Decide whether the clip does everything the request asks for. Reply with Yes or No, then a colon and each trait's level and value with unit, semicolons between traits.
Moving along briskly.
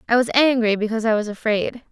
Yes: fast, 220 wpm